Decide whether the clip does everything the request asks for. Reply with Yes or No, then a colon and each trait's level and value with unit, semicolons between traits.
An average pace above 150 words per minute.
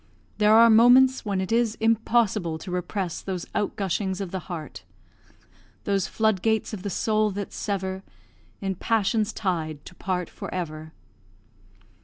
No: average, 145 wpm